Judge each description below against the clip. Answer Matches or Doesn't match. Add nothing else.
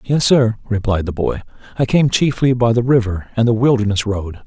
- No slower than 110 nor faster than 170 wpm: Doesn't match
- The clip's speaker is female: Doesn't match